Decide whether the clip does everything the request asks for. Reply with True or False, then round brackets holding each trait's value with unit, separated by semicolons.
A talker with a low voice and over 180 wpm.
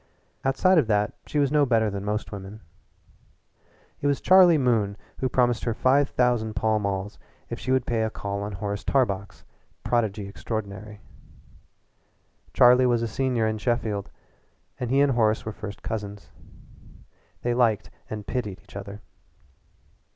False (110 Hz; 150 wpm)